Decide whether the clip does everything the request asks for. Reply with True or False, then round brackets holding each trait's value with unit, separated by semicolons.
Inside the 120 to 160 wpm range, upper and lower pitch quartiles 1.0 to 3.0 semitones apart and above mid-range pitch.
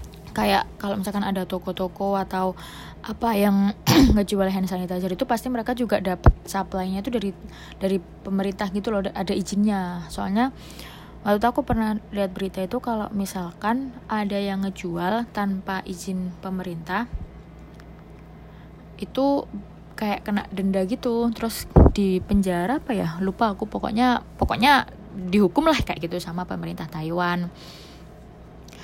True (125 wpm; 2.7 semitones; 195 Hz)